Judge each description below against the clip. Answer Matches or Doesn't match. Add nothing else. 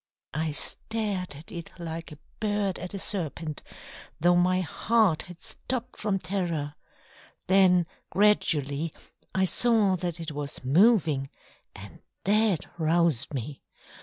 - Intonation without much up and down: Doesn't match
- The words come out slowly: Matches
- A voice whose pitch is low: Doesn't match